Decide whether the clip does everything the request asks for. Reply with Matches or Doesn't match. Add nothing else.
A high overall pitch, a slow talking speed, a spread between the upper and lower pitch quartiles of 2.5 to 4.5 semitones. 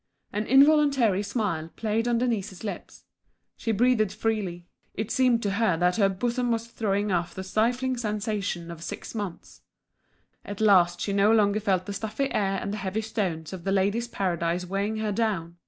Doesn't match